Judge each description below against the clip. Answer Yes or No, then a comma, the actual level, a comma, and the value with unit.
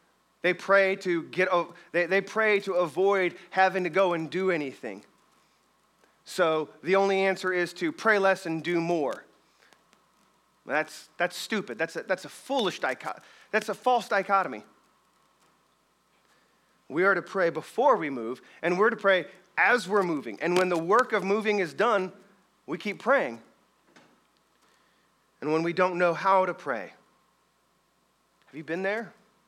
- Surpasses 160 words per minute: No, average, 155 wpm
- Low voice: No, high, 190 Hz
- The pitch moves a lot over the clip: No, narrow, 2.4 semitones